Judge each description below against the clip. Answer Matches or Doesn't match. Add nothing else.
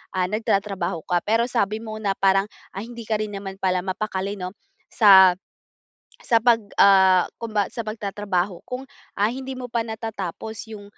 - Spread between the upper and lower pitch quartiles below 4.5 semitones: Matches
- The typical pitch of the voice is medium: Doesn't match